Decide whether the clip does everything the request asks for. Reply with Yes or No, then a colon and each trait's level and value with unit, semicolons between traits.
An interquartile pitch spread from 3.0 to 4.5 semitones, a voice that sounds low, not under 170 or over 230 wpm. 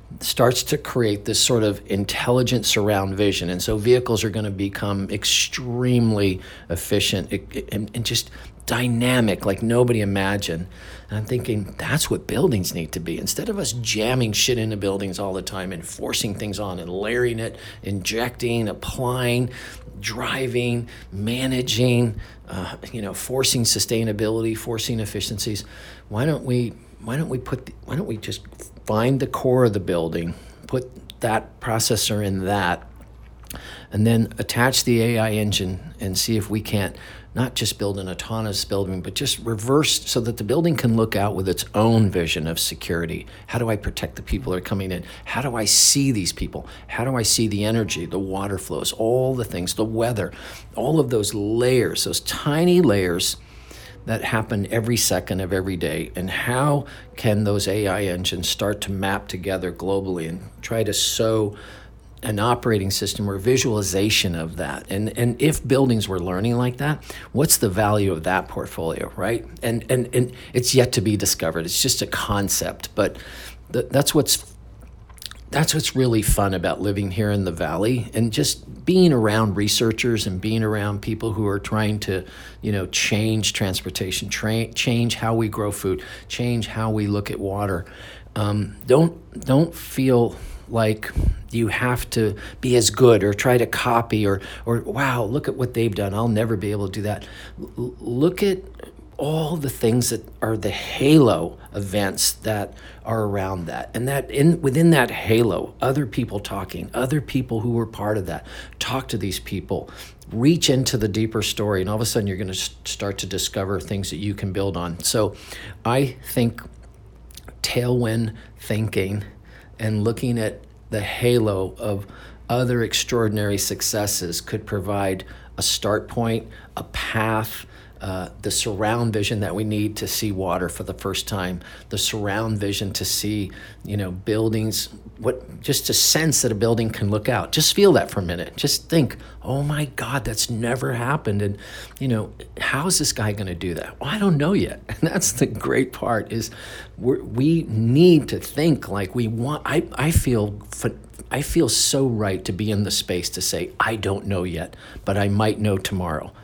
Yes: average, 3.4 semitones; low, 110 Hz; average, 175 wpm